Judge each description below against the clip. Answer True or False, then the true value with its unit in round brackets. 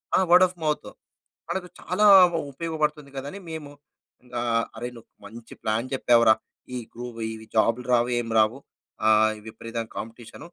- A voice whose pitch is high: False (120 Hz)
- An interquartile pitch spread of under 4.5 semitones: False (4.8 semitones)